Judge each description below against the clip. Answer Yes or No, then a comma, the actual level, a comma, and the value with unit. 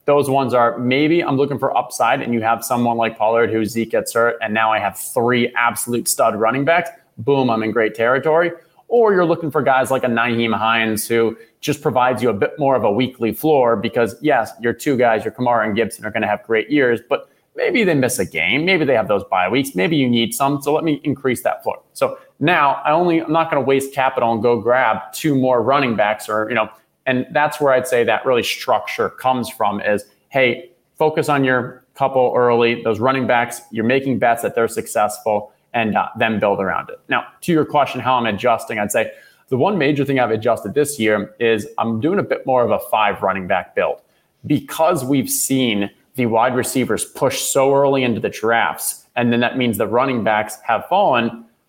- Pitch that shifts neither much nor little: Yes, average, 3.5 semitones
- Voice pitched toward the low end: Yes, low, 125 Hz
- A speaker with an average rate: No, fast, 220 wpm